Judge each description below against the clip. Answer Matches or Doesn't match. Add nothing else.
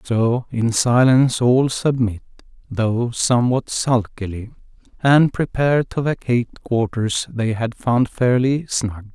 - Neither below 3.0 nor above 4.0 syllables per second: Matches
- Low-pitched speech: Matches